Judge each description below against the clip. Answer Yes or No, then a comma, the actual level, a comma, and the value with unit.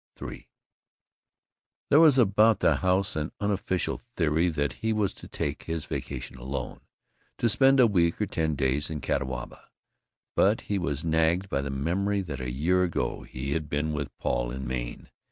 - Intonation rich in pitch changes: Yes, wide, 6.1 semitones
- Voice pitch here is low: Yes, very low, 80 Hz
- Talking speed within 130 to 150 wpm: No, average, 170 wpm